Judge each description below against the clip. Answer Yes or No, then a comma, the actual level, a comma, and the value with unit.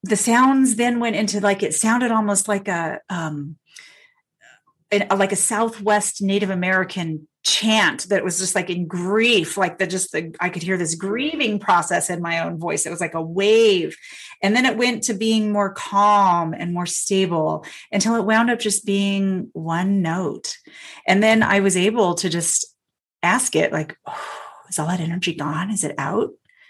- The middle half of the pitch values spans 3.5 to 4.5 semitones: Yes, average, 3.8 semitones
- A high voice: Yes, high, 200 Hz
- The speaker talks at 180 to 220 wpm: Yes, average, 185 wpm